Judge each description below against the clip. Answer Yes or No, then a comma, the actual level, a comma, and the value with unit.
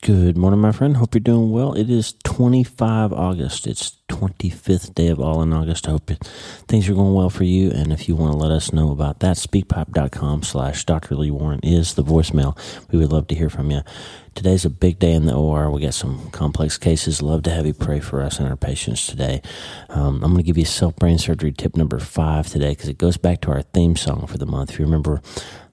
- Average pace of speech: No, fast, 235 wpm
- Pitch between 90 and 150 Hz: No, very low, 80 Hz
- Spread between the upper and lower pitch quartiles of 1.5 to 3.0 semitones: No, average, 3.8 semitones